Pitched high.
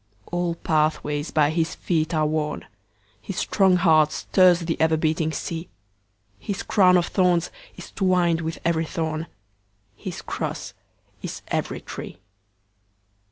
No: medium, 160 Hz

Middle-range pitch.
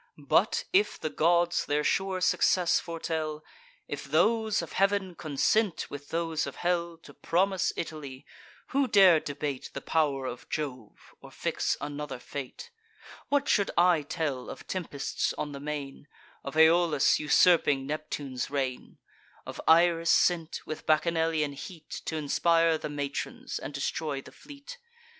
Yes: medium, 160 Hz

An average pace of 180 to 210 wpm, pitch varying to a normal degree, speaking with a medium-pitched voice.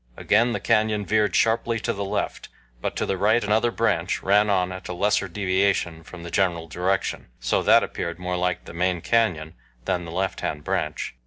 No: average, 190 wpm; average, 3.3 semitones; very low, 95 Hz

